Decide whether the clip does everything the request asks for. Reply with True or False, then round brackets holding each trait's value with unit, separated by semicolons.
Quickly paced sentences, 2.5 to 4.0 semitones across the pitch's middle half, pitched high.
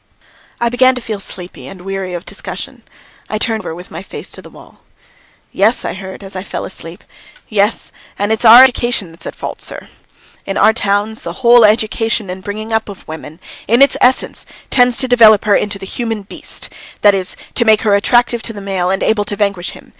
True (210 wpm; 3.0 semitones; 210 Hz)